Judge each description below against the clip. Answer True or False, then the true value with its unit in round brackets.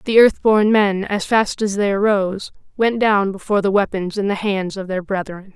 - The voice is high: True (200 Hz)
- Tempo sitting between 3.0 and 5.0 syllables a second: True (4.9 syllables/s)